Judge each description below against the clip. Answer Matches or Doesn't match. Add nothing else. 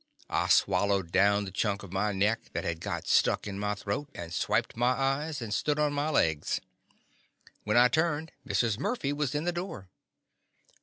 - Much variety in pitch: Matches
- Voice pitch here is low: Matches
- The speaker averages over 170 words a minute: Matches